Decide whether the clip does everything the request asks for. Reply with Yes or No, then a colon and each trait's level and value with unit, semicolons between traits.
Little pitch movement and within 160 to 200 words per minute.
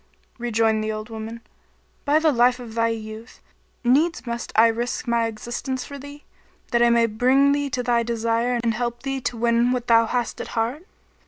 Yes: narrow, 1.8 semitones; average, 190 wpm